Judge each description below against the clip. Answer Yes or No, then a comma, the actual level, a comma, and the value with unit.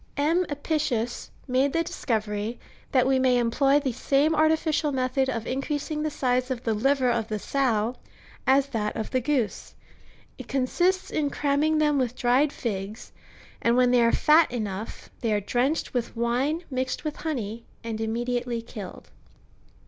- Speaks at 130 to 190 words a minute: Yes, average, 170 wpm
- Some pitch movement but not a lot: Yes, average, 3.8 semitones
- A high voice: Yes, very high, 255 Hz